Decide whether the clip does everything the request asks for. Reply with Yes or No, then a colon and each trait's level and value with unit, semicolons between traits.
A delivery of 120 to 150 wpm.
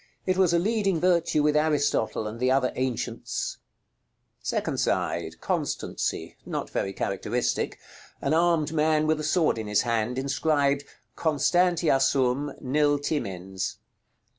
Yes: average, 140 wpm